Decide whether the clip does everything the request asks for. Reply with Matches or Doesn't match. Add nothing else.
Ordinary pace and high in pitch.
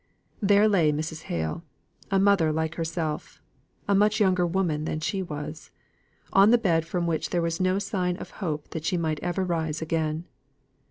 Doesn't match